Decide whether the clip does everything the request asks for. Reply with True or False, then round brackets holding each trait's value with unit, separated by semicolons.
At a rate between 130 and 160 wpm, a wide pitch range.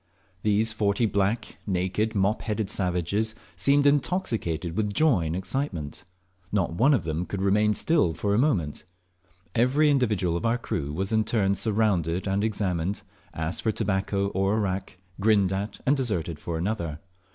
False (155 wpm; 3.6 semitones)